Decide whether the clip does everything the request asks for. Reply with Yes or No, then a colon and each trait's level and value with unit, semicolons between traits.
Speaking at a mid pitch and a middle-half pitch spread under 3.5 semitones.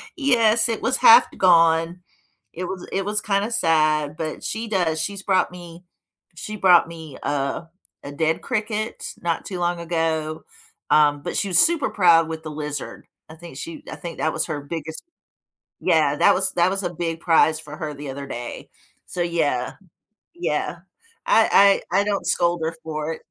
No: medium, 170 Hz; average, 3.8 semitones